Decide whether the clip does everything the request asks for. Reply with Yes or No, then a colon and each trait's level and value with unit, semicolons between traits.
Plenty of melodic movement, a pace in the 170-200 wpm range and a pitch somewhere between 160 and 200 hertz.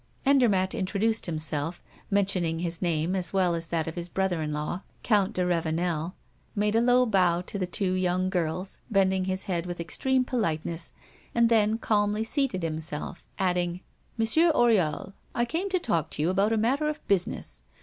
No: average, 4.4 semitones; average, 175 wpm; medium, 185 Hz